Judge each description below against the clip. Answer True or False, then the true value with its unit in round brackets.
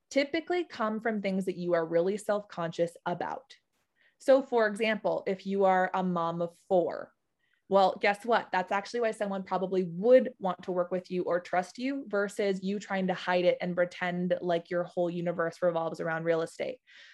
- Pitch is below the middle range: False (190 Hz)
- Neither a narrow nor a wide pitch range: True (3.7 semitones)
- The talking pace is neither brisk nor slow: True (190 wpm)